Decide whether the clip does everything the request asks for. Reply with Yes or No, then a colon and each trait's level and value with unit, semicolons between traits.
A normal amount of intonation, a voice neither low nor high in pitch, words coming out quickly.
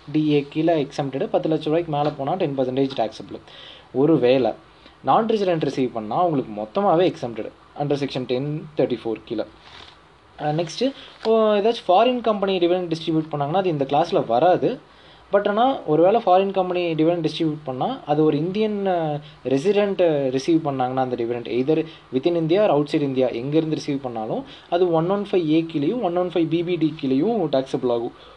Yes: average, 4.6 semitones; medium, 155 Hz; fast, 160 wpm